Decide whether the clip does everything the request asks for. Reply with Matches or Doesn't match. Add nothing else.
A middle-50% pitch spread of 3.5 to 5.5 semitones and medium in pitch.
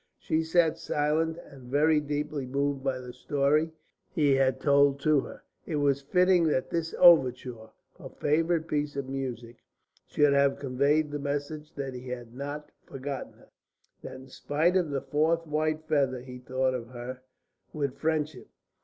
Doesn't match